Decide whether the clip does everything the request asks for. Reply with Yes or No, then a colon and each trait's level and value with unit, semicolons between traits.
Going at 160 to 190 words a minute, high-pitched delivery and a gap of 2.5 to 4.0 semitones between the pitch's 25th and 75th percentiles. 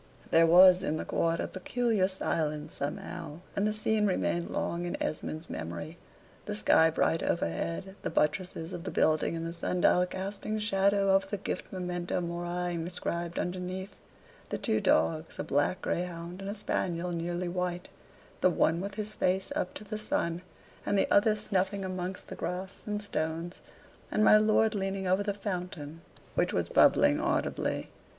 No: average, 170 wpm; medium, 180 Hz; average, 2.8 semitones